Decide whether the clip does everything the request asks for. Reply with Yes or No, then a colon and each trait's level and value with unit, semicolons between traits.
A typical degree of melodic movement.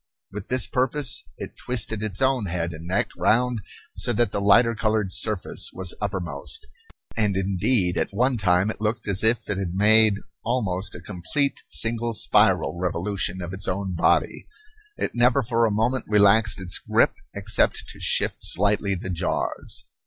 Yes: average, 3.7 semitones